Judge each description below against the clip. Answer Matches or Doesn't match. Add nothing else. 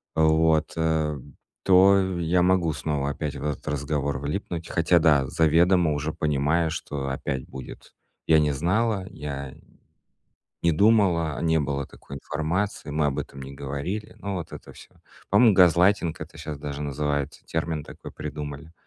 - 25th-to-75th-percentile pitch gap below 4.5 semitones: Matches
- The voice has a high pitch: Doesn't match